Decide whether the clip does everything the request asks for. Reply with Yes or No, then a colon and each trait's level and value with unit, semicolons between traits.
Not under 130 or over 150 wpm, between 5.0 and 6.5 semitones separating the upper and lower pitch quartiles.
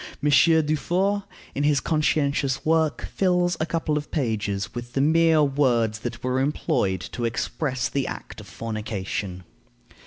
Yes: average, 145 wpm; average, 5.3 semitones